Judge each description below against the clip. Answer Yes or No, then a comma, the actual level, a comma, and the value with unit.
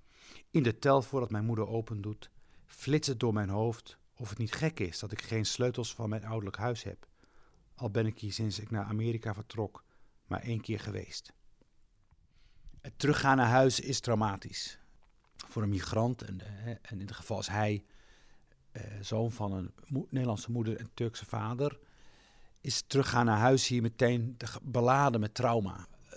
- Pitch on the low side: Yes, low, 115 Hz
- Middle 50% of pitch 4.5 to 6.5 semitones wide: No, average, 2.7 semitones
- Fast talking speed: No, average, 165 wpm